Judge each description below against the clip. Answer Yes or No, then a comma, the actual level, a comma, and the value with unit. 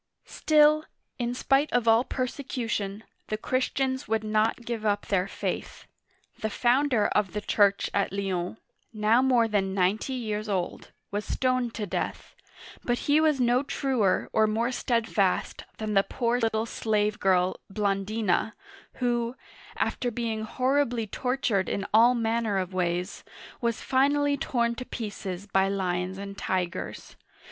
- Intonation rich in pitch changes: No, average, 3.7 semitones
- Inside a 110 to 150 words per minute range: Yes, average, 145 wpm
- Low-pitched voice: No, high, 220 Hz